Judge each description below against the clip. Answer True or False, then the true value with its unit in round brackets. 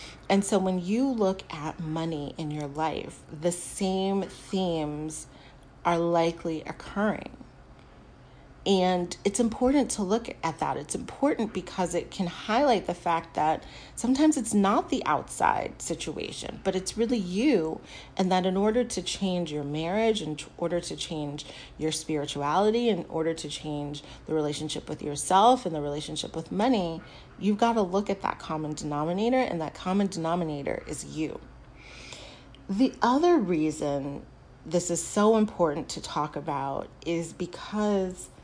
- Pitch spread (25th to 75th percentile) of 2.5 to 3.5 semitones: False (4.6 semitones)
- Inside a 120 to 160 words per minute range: True (150 wpm)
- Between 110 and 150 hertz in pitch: False (170 Hz)